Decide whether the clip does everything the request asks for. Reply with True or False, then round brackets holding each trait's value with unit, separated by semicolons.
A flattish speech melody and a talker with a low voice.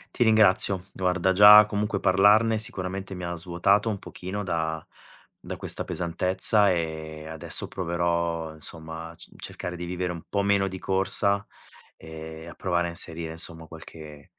False (3.1 semitones; 90 Hz)